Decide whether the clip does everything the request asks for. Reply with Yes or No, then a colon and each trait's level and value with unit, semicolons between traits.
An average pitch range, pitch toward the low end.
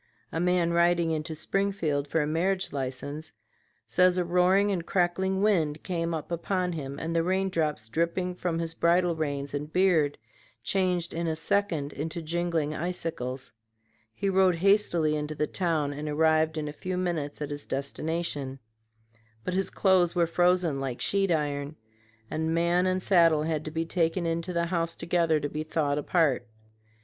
No: average, 3.0 semitones; medium, 165 Hz